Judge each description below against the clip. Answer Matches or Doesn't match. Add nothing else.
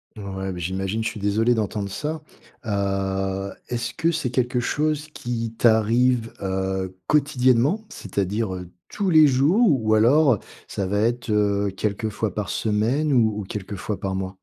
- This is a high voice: Doesn't match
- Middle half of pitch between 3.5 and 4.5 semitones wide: Matches